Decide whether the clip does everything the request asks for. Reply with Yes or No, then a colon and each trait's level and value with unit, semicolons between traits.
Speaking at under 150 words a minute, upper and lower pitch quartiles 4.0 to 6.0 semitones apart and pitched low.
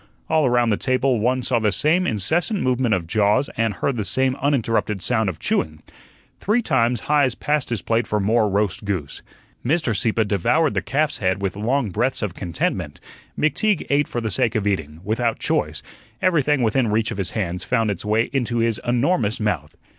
No: average, 190 wpm; average, 4.4 semitones; low, 115 Hz